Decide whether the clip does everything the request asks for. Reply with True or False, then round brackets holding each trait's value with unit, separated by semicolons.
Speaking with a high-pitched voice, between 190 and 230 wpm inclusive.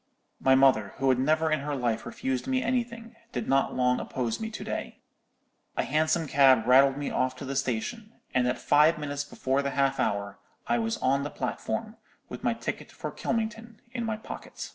False (140 Hz; 195 wpm)